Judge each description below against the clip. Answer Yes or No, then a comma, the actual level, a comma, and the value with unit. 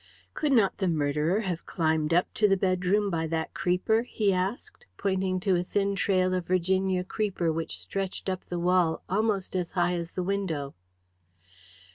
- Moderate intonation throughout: No, narrow, 2.3 semitones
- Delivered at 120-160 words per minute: No, average, 170 wpm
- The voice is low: No, medium, 185 Hz